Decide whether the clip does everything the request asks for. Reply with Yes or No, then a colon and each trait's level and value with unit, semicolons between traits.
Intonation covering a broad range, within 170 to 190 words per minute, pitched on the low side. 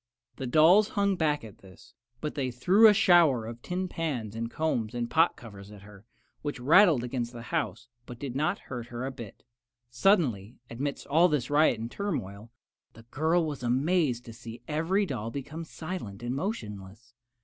Yes: wide, 5.9 semitones; average, 180 wpm; low, 130 Hz